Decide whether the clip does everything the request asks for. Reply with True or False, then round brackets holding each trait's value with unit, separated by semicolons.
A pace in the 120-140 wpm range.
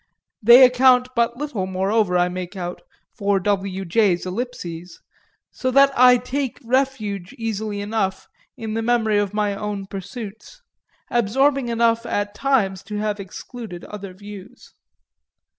True (135 wpm)